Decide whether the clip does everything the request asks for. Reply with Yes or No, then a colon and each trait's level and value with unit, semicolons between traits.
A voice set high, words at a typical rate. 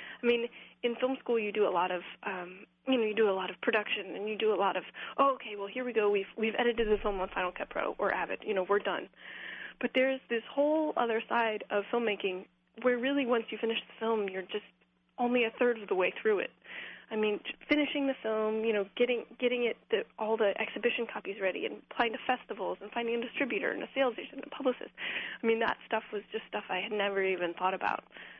No: high, 225 Hz; fast, 245 wpm